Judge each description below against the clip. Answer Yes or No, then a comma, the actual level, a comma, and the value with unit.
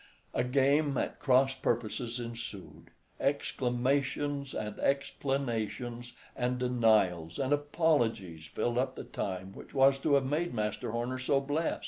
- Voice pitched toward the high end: No, low, 125 Hz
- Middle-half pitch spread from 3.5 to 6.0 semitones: No, average, 3.1 semitones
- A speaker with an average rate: No, slow, 130 wpm